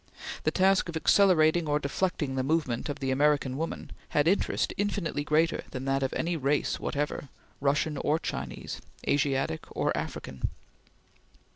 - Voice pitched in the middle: Yes, medium, 150 Hz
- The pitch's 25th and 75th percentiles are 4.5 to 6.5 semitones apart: No, average, 3.3 semitones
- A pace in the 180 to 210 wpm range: No, average, 145 wpm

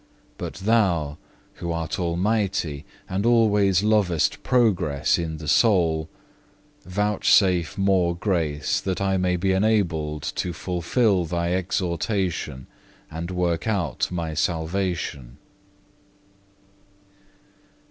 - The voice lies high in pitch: No, very low, 90 Hz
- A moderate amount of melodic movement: Yes, average, 3.3 semitones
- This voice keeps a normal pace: No, slow, 95 wpm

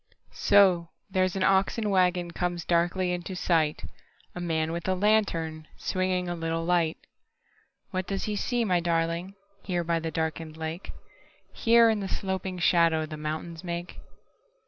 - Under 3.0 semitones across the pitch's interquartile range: Yes, narrow, 2.4 semitones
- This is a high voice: No, medium, 175 Hz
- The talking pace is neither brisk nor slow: No, slow, 125 wpm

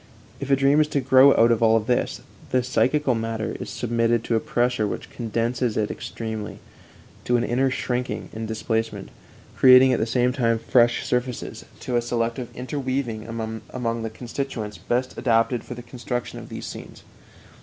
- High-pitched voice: No, low, 120 Hz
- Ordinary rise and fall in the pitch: No, narrow, 2.0 semitones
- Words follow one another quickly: No, average, 170 wpm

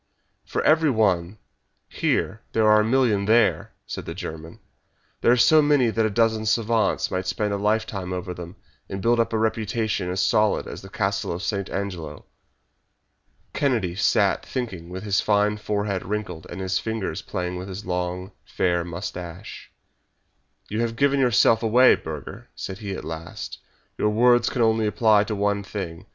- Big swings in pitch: No, average, 3.4 semitones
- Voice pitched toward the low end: Yes, low, 105 Hz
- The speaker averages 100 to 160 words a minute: No, average, 170 wpm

